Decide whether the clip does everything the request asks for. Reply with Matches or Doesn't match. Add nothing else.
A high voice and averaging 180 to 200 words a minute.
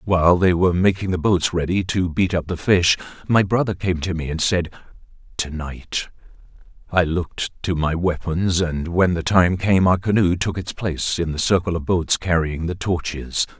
Doesn't match